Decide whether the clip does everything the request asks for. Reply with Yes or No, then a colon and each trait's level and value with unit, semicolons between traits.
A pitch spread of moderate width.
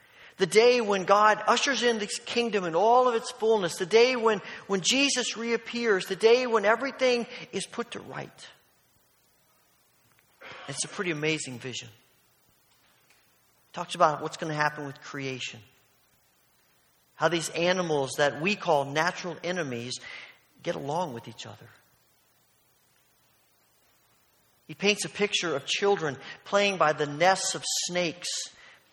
No: wide, 6.8 semitones